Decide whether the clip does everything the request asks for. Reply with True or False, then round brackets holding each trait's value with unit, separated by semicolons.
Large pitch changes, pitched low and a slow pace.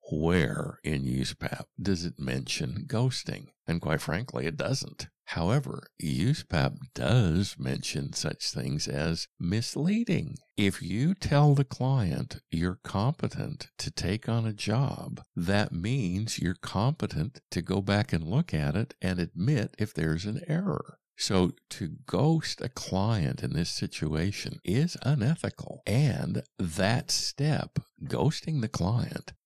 True (8.1 semitones; 105 Hz; 130 wpm)